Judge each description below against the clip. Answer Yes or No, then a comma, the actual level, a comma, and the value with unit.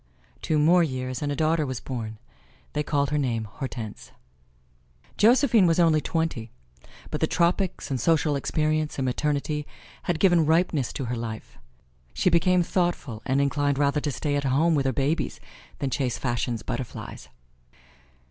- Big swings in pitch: No, average, 4.0 semitones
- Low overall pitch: No, medium, 145 Hz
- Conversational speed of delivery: Yes, average, 155 wpm